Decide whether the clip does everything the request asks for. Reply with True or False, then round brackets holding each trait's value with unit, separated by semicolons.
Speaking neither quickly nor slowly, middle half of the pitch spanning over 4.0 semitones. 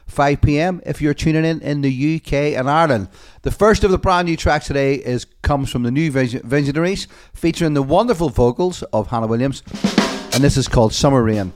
True (195 wpm; 4.5 semitones)